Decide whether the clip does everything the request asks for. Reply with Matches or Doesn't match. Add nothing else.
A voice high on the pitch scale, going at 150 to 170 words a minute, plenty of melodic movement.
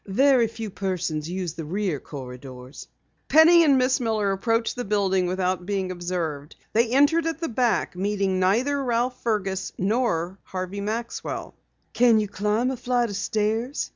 Doesn't match